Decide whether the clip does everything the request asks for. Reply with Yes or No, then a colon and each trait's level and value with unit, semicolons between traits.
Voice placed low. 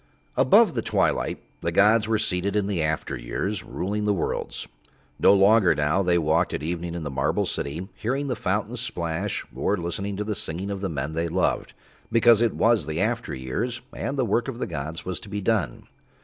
Yes: very low, 95 Hz